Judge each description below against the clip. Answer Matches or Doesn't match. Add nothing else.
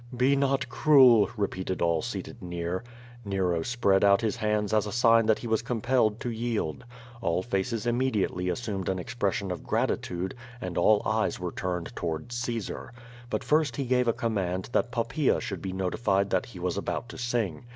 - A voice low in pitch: Matches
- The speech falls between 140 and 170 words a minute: Doesn't match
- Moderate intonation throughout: Matches